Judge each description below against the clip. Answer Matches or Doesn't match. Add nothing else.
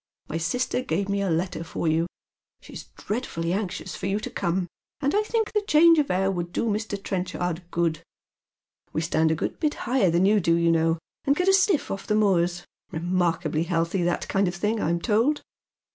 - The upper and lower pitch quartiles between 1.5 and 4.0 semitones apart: Doesn't match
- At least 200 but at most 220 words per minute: Matches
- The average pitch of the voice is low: Doesn't match